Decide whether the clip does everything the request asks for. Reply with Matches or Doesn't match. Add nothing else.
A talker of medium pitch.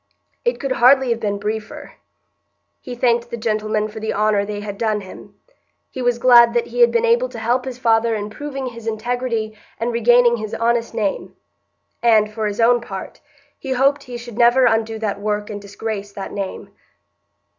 Doesn't match